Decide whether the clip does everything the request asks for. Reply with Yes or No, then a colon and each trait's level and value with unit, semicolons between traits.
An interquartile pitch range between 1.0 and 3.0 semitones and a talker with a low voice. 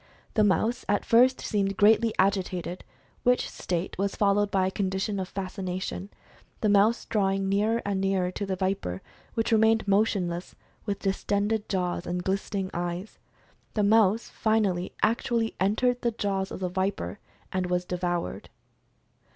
No: narrow, 2.4 semitones; high, 195 Hz